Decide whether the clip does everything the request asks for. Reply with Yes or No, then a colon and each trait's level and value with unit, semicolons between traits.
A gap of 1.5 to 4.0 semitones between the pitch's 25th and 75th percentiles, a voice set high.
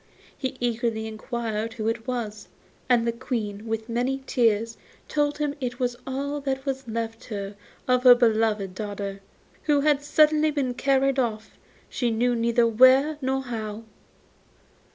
Yes: average, 3.2 semitones; high, 240 Hz